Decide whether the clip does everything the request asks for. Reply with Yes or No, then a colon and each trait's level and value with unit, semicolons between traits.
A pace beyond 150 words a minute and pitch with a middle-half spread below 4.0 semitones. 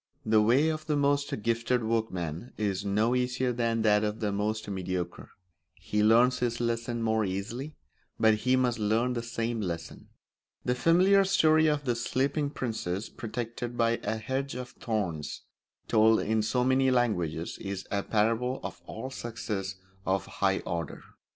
Yes: average, 160 wpm; average, 3.1 semitones